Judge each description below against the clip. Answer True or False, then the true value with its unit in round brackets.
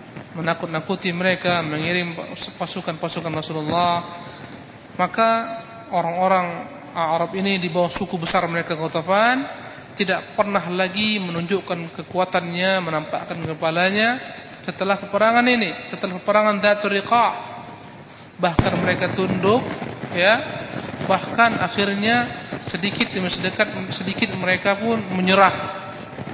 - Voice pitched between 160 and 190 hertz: True (185 Hz)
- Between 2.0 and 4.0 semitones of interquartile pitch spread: True (2.7 semitones)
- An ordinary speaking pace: True (95 wpm)